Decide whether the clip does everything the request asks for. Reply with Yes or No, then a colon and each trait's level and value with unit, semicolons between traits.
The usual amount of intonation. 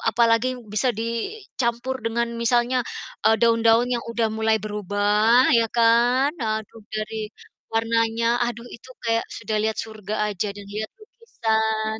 No: narrow, 1.4 semitones